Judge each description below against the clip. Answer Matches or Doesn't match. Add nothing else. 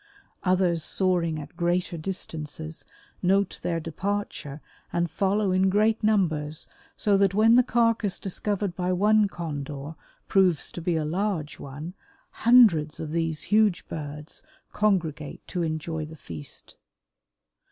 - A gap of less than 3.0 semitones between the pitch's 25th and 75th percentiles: Doesn't match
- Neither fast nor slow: Doesn't match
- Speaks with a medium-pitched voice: Matches